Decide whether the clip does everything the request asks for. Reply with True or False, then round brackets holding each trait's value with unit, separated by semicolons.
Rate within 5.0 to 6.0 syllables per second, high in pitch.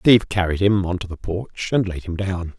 False (5.1 syllables/s; 95 Hz)